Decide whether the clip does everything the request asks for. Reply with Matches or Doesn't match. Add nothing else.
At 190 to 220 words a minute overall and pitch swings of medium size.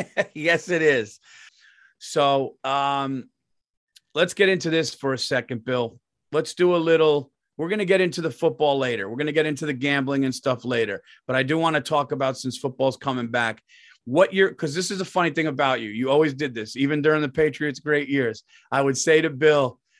Matches